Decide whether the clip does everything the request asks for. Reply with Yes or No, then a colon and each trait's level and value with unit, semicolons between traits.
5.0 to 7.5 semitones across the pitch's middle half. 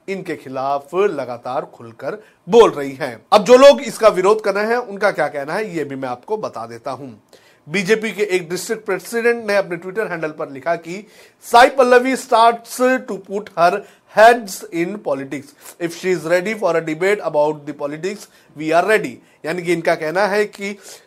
Yes: wide, 5.5 semitones